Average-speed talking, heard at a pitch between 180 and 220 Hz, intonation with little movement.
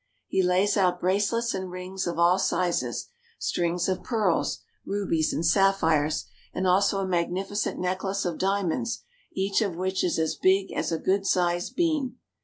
Yes: average, 160 wpm; medium, 185 Hz; narrow, 2.1 semitones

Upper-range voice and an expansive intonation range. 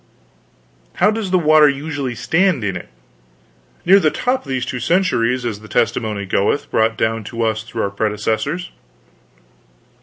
No: low, 125 Hz; wide, 6.5 semitones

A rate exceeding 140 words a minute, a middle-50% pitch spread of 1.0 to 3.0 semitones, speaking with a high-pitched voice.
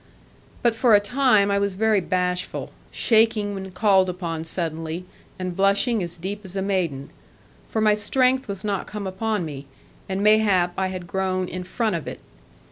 Yes: average, 175 wpm; average, 2.7 semitones; high, 195 Hz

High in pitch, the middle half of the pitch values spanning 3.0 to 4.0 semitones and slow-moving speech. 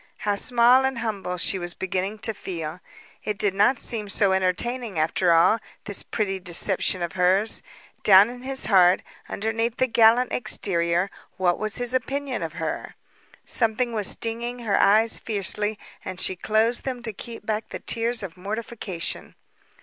No: high, 215 Hz; average, 3.7 semitones; average, 160 wpm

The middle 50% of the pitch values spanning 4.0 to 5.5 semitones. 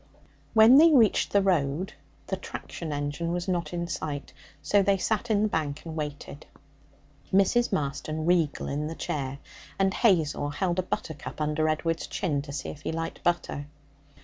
Yes: average, 4.5 semitones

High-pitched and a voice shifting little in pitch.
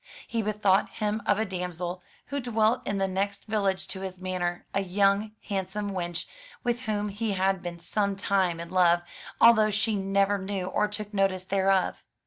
Yes: high, 195 Hz; narrow, 2.1 semitones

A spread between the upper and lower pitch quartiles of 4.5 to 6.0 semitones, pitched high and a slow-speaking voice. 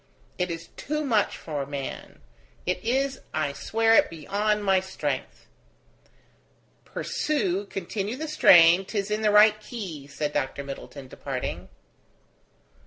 Yes: wide, 5.6 semitones; high, 195 Hz; slow, 125 wpm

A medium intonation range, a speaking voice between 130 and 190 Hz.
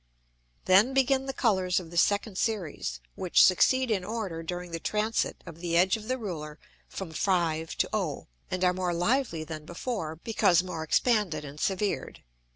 Yes: average, 4.7 semitones; medium, 185 Hz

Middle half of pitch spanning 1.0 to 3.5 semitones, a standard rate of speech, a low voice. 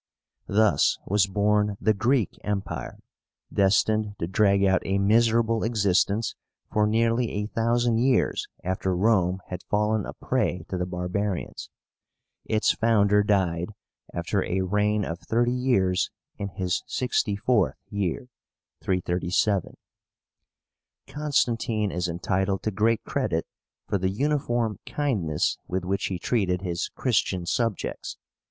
No: average, 3.2 semitones; slow, 125 wpm; low, 105 Hz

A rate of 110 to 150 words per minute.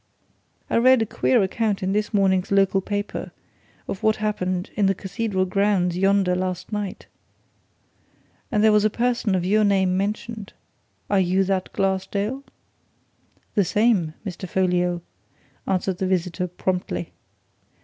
Yes: average, 140 wpm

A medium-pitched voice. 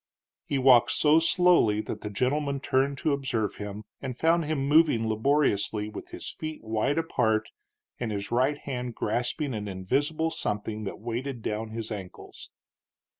No: low, 125 Hz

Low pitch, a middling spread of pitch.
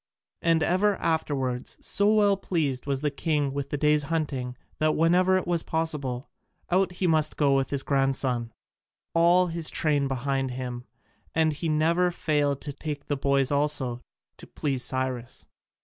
No: medium, 145 Hz; average, 3.5 semitones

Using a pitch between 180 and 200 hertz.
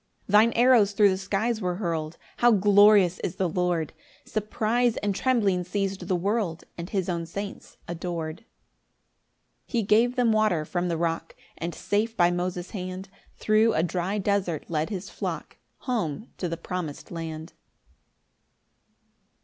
Yes: high, 190 Hz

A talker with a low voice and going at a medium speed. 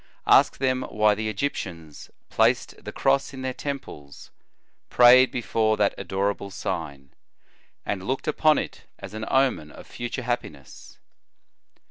No: low, 110 Hz; slow, 130 wpm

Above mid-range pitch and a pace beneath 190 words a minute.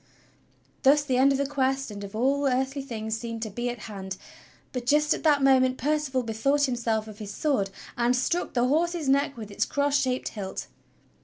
No: very high, 260 Hz; average, 200 wpm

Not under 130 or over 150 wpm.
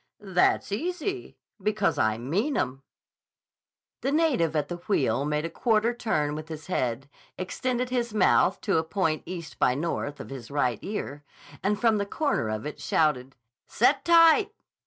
No: average, 160 wpm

